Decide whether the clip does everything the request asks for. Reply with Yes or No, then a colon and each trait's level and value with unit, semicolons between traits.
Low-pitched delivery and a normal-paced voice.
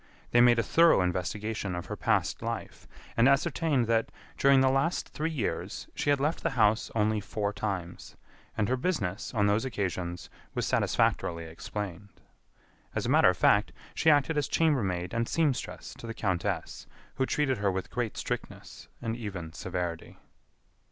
Yes: low, 110 Hz; average, 165 wpm